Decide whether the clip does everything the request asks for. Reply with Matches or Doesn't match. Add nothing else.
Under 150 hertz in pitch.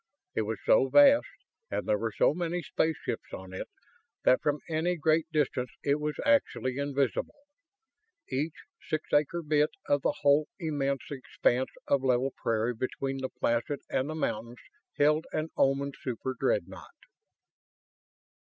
Matches